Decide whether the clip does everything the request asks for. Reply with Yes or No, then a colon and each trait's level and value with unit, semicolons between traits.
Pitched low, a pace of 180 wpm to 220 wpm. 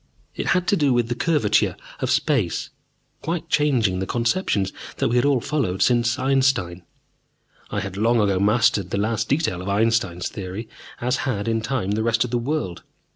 Yes: low, 115 Hz; average, 185 wpm